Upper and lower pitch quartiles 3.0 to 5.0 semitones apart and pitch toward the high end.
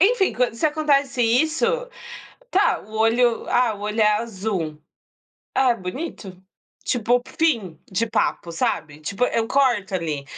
No: wide, 5.5 semitones; high, 230 Hz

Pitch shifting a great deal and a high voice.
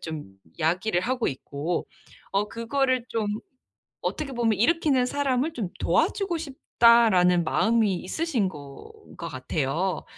Yes: wide, 6.7 semitones; high, 225 Hz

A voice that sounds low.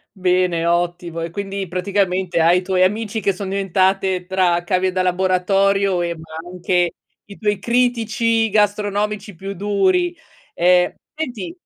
No: high, 190 Hz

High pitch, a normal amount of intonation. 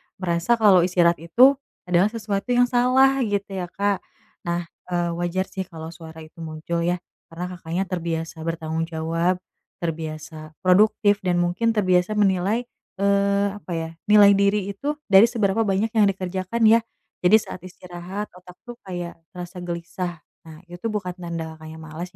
No: medium, 180 Hz; average, 3.1 semitones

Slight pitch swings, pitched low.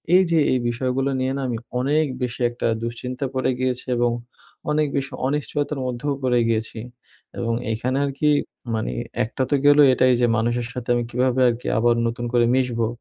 Yes: narrow, 2.2 semitones; low, 125 Hz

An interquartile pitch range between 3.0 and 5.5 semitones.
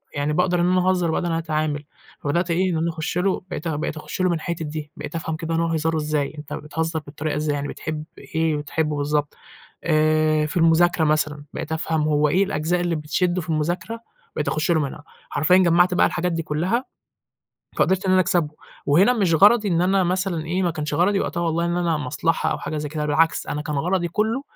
No: narrow, 2.6 semitones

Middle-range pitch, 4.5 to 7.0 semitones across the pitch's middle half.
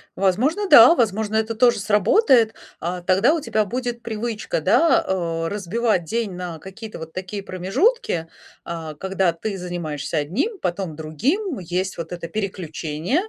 No: high, 195 Hz; average, 5.3 semitones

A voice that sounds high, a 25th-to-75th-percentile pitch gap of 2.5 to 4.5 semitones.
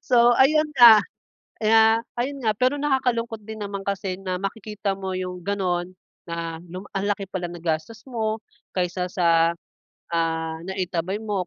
Yes: high, 195 Hz; average, 3.9 semitones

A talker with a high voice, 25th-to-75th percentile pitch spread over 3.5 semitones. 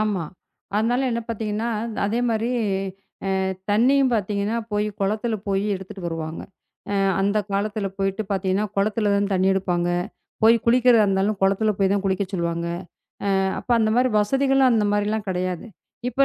No: high, 205 Hz; average, 2.7 semitones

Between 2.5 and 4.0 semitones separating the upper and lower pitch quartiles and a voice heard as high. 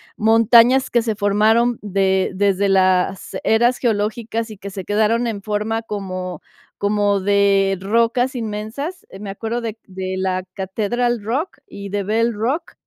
Yes: average, 2.8 semitones; high, 210 Hz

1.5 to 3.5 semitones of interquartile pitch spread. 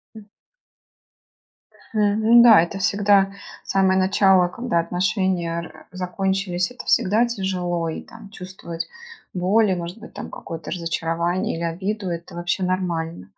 Yes: average, 2.8 semitones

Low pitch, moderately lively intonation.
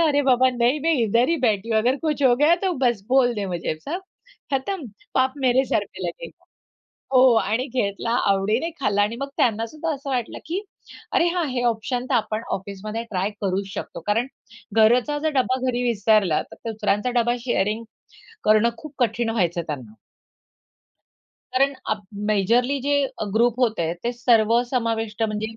No: high, 235 Hz; average, 3.5 semitones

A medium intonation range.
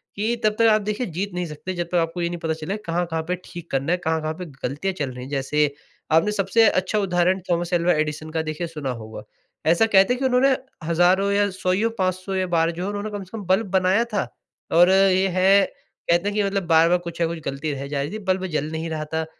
Yes: average, 3.5 semitones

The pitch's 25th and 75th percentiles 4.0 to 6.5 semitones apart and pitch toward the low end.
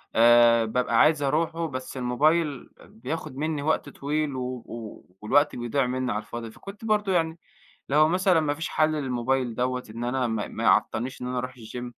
Yes: average, 4.3 semitones; low, 130 Hz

